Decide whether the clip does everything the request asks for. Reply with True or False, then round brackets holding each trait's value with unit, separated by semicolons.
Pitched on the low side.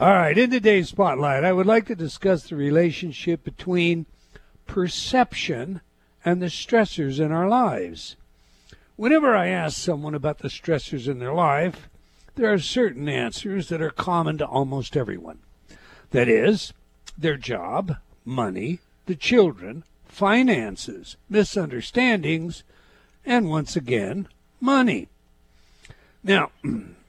False (170 Hz)